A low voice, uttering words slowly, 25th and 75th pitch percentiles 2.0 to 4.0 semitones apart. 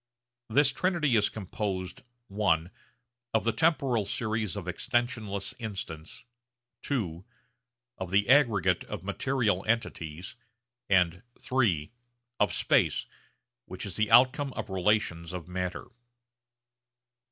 No: low, 105 Hz; slow, 105 wpm; average, 4.5 semitones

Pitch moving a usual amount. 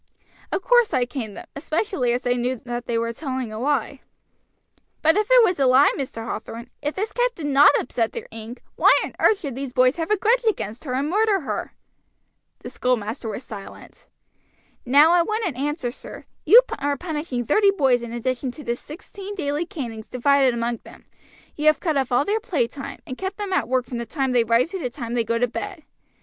No: wide, 6.0 semitones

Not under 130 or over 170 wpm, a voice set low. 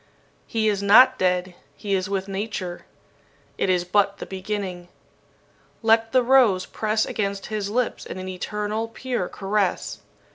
No: average, 145 wpm; high, 200 Hz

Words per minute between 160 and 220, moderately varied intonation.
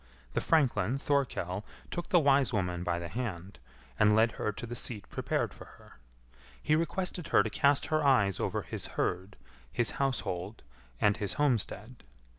No: average, 165 wpm; wide, 6.0 semitones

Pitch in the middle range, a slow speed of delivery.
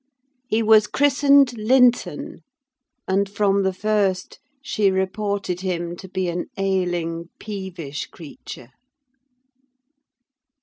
No: high, 195 Hz; slow, 95 wpm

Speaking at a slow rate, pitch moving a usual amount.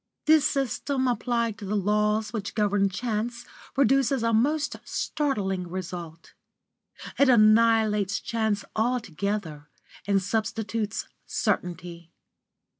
Yes: slow, 100 wpm; average, 3.5 semitones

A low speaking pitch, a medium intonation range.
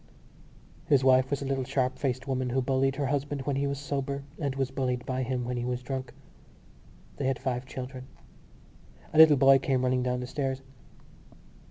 No: low, 130 Hz; narrow, 1.3 semitones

